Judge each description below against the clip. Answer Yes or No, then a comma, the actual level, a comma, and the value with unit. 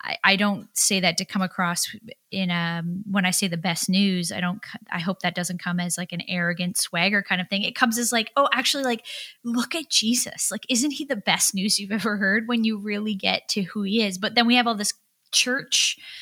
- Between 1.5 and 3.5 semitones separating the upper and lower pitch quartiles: No, average, 4.3 semitones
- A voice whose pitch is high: Yes, high, 200 Hz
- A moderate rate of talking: No, fast, 235 wpm